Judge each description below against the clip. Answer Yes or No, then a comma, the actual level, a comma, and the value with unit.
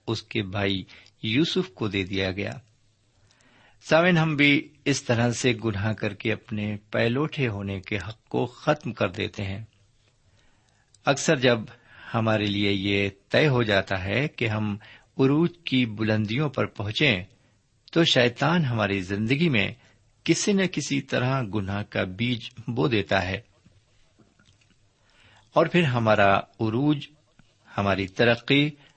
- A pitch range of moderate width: Yes, average, 4.5 semitones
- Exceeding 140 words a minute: No, average, 135 wpm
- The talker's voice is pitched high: No, low, 110 Hz